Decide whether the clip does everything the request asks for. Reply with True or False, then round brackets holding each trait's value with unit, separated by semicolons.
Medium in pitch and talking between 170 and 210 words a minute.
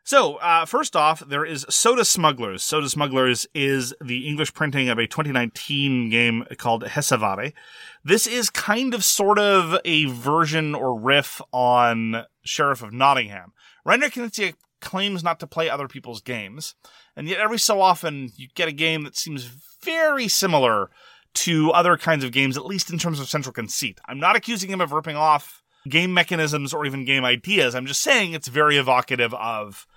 True (150 Hz; 175 wpm)